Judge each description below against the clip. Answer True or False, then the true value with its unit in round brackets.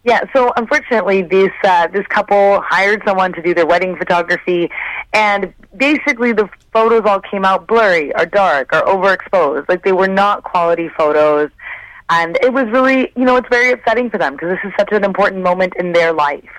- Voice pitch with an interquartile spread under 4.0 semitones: False (4.5 semitones)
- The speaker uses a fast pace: False (190 wpm)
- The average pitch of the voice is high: True (200 Hz)